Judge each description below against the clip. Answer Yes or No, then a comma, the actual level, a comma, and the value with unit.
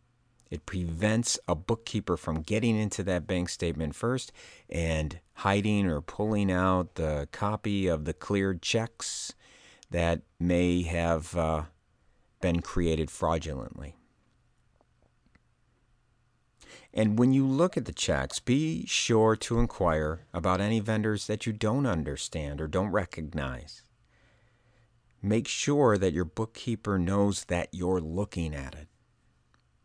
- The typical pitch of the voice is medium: No, low, 100 Hz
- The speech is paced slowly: Yes, slow, 125 wpm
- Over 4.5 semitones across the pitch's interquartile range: Yes, average, 5.3 semitones